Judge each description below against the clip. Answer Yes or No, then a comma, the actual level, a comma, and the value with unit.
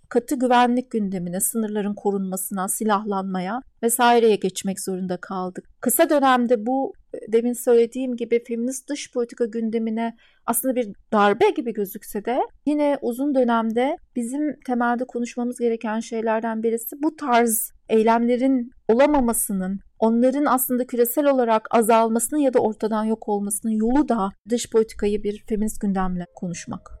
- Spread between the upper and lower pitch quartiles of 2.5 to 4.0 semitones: Yes, average, 2.8 semitones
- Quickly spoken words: No, average, 125 wpm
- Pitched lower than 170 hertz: No, high, 230 Hz